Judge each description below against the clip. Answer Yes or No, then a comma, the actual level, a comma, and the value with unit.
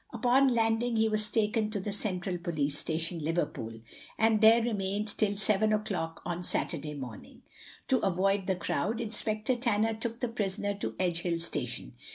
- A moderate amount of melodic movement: Yes, average, 4.3 semitones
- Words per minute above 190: No, average, 160 wpm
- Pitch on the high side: Yes, high, 205 Hz